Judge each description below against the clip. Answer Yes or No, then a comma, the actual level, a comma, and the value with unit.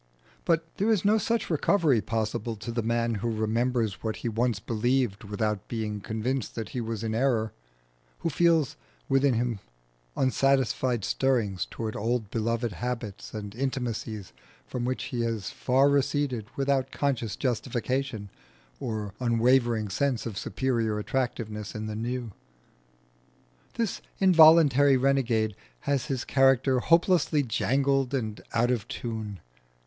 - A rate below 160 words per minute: Yes, slow, 135 wpm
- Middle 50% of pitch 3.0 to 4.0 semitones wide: Yes, average, 3.5 semitones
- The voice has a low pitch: Yes, low, 120 Hz